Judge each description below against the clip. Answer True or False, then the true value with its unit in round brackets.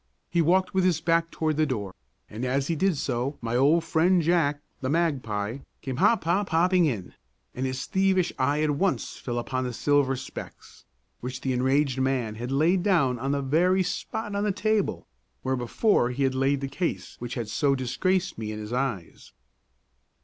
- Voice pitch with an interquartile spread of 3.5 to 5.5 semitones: True (5.2 semitones)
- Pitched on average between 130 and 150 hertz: True (140 Hz)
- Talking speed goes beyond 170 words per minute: True (190 wpm)